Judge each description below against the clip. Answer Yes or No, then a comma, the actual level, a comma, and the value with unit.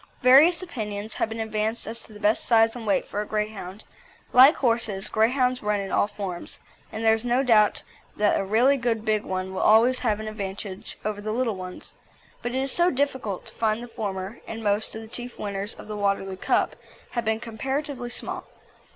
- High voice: Yes, high, 220 Hz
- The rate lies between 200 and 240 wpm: Yes, fast, 205 wpm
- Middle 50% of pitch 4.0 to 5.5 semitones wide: No, average, 2.8 semitones